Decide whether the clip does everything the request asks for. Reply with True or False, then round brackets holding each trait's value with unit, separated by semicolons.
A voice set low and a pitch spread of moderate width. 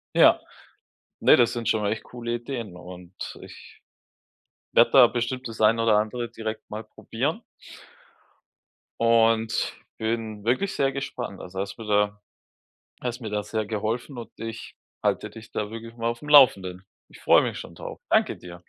False (115 Hz; 2.1 semitones)